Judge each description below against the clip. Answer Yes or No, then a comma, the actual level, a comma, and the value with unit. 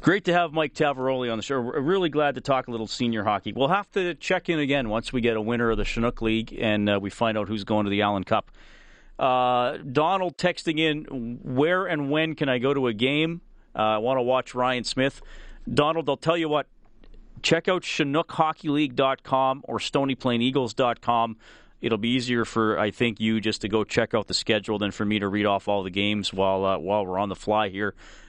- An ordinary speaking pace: No, fast, 220 wpm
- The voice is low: Yes, low, 125 Hz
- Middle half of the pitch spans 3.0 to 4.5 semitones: No, average, 5.3 semitones